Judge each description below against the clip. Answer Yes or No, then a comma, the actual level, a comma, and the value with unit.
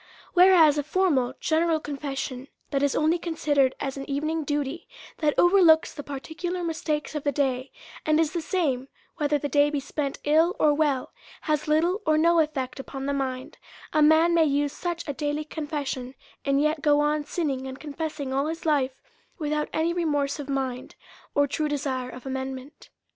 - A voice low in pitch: No, very high, 295 Hz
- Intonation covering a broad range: No, narrow, 2.5 semitones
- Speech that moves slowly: No, average, 180 wpm